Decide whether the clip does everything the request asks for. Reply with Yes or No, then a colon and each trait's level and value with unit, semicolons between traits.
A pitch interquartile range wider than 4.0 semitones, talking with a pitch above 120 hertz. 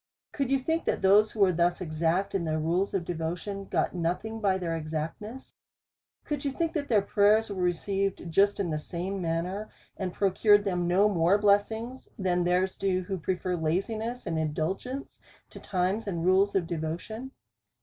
No: average, 3.4 semitones; high, 190 Hz